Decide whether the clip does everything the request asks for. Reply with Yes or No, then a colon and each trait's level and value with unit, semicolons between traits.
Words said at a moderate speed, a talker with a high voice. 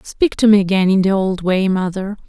No: fast, 235 wpm; high, 195 Hz